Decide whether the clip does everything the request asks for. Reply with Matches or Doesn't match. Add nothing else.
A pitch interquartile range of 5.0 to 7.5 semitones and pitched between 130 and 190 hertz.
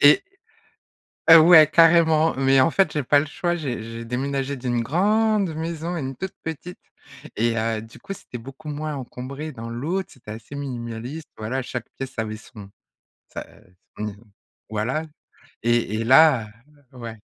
Matches